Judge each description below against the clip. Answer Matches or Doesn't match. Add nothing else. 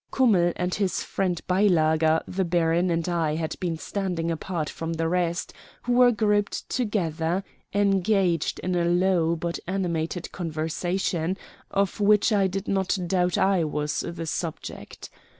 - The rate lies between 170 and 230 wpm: Doesn't match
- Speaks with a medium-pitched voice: Matches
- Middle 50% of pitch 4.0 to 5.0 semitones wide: Doesn't match